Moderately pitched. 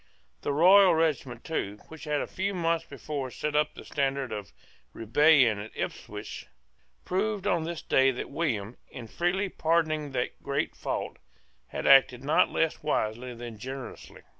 Yes: medium, 145 Hz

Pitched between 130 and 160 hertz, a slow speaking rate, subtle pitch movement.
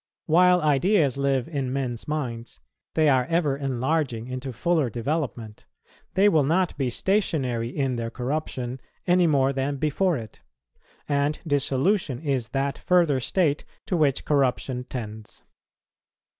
No: medium, 140 Hz; slow, 130 wpm; average, 3.8 semitones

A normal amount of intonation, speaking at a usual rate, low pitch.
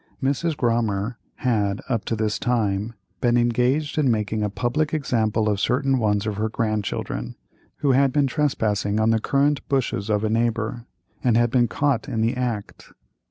Yes: average, 3.5 semitones; average, 170 wpm; low, 115 Hz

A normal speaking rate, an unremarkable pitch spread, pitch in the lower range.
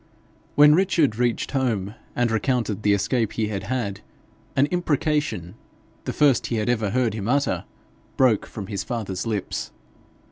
Yes: average, 150 wpm; average, 4.2 semitones; low, 115 Hz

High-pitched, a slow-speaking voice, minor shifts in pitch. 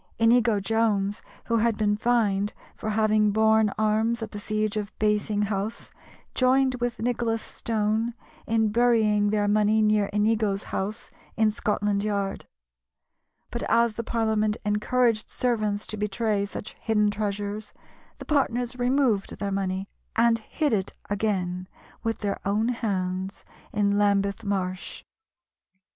Yes: high, 215 Hz; slow, 130 wpm; narrow, 1.8 semitones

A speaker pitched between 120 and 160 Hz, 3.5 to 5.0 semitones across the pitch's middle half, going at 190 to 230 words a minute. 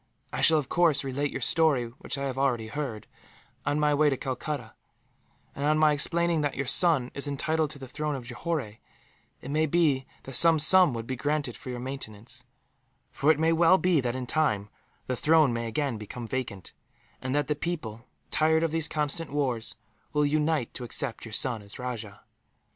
Yes: medium, 140 Hz; average, 3.9 semitones; average, 195 wpm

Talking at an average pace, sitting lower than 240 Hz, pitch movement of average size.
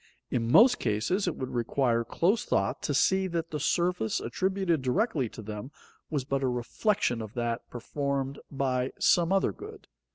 No: average, 165 wpm; low, 135 Hz; wide, 6.9 semitones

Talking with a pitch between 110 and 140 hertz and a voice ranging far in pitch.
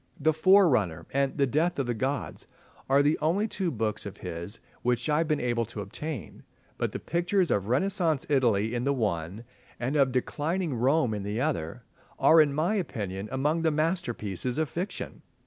Yes: low, 135 Hz; wide, 6.0 semitones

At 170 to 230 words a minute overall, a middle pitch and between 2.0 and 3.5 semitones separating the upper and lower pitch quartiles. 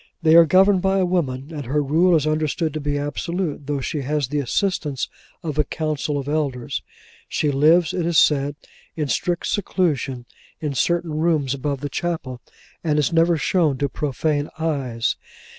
Yes: average, 175 wpm; medium, 150 Hz; average, 3.0 semitones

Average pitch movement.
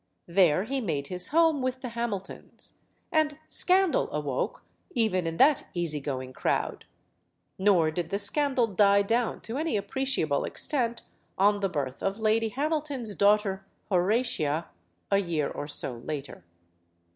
No: wide, 7.5 semitones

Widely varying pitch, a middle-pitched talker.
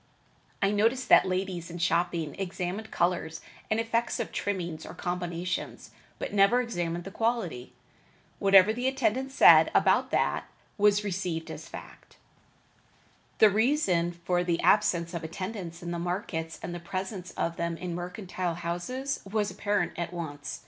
No: average, 3.4 semitones; medium, 180 Hz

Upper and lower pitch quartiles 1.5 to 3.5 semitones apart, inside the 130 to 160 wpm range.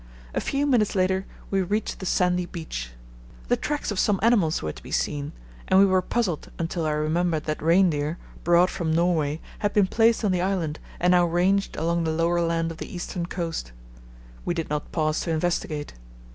No: average, 2.9 semitones; average, 195 wpm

